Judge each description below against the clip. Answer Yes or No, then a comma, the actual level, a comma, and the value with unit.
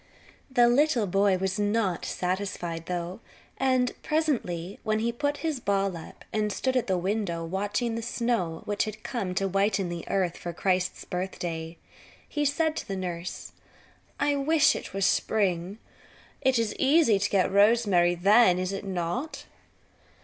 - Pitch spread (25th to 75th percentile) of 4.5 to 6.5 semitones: Yes, average, 4.8 semitones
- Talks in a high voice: Yes, high, 200 Hz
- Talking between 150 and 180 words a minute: Yes, average, 160 wpm